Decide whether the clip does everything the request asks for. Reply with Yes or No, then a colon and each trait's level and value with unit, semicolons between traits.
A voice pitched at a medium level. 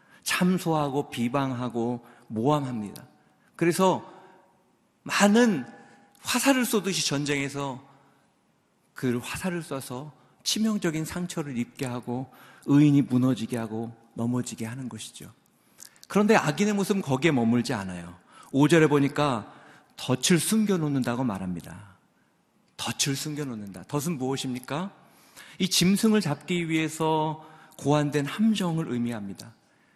Yes: medium, 145 Hz